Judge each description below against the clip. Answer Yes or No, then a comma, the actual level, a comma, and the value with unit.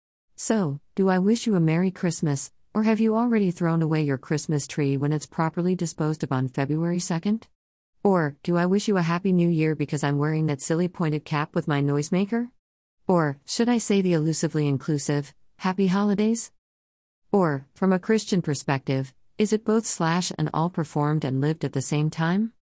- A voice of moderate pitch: Yes, medium, 165 Hz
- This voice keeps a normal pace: Yes, average, 190 wpm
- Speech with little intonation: No, average, 4.6 semitones